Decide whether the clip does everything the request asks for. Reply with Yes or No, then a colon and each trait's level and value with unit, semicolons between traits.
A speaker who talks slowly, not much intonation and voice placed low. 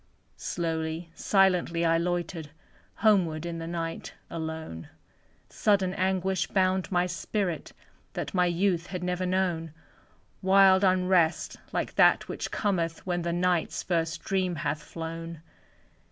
No: slow, 125 wpm; narrow, 2.2 semitones; medium, 175 Hz